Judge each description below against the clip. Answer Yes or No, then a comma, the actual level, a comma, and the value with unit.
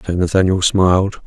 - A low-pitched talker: Yes, very low, 95 Hz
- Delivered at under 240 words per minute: Yes, average, 140 wpm